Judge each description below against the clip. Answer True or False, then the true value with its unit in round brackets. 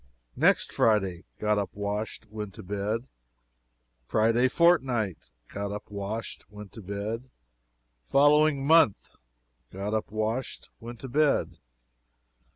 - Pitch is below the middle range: True (110 Hz)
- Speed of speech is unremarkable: False (115 wpm)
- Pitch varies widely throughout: False (3.9 semitones)